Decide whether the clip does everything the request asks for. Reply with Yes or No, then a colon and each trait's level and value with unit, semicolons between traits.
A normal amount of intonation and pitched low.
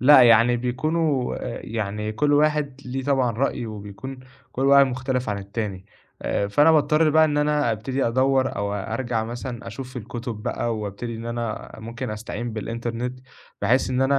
Yes: average, 3.3 semitones; low, 120 Hz